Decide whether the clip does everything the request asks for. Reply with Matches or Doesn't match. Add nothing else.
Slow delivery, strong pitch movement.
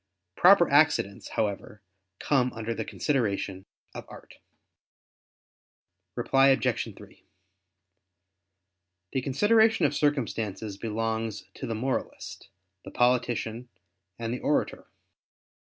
Doesn't match